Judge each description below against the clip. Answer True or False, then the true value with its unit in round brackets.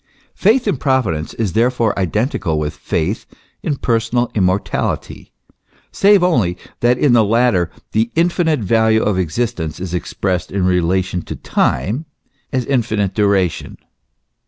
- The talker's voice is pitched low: True (110 Hz)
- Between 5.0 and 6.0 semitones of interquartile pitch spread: True (5.3 semitones)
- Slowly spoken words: True (130 wpm)